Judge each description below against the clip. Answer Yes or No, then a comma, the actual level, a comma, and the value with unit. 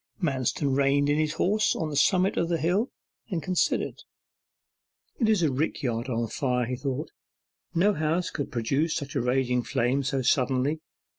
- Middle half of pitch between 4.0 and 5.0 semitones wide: Yes, average, 4.5 semitones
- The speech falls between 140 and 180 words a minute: Yes, average, 170 wpm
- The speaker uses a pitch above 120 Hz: Yes, medium, 140 Hz